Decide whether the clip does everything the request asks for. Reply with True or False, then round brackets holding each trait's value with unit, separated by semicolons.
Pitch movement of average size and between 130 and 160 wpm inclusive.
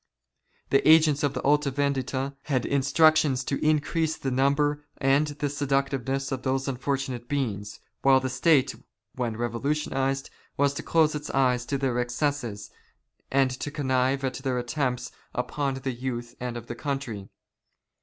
False (2.2 semitones; 145 wpm)